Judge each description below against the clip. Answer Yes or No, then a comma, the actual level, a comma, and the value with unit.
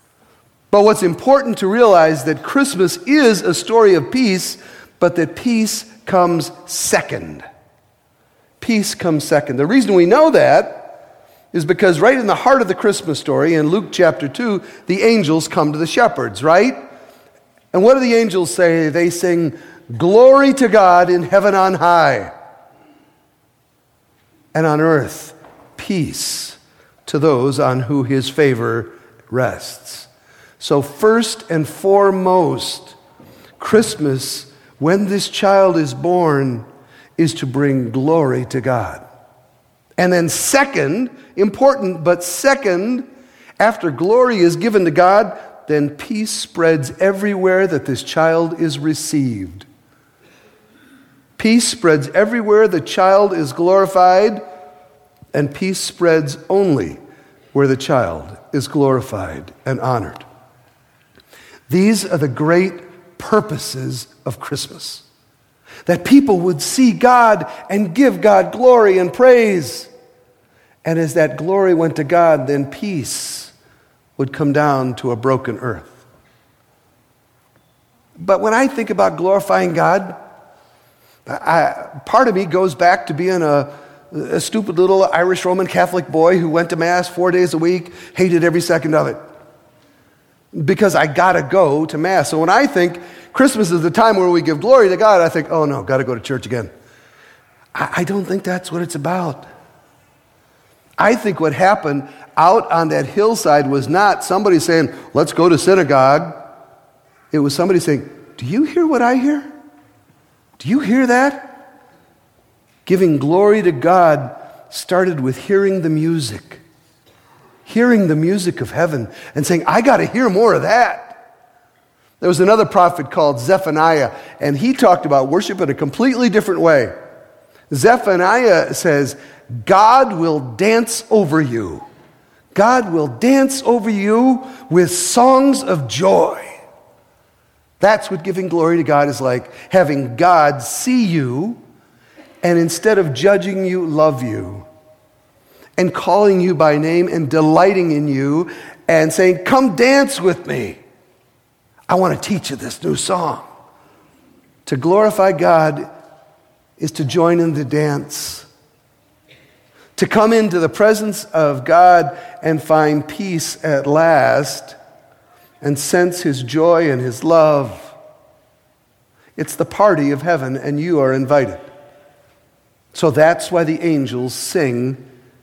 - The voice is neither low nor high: Yes, medium, 170 Hz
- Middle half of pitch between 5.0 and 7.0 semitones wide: Yes, average, 5.3 semitones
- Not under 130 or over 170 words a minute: Yes, average, 140 wpm